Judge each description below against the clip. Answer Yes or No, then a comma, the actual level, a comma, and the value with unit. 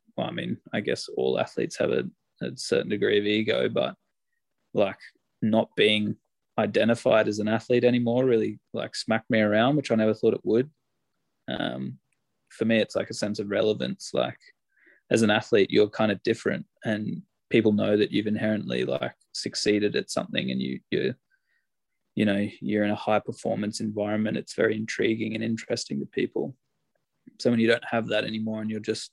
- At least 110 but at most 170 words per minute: No, average, 185 wpm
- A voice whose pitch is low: Yes, low, 110 Hz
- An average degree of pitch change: No, narrow, 1.3 semitones